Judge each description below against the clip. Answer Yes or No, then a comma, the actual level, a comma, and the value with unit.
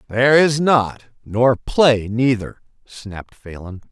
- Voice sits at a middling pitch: No, low, 120 Hz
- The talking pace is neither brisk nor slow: No, slow, 125 wpm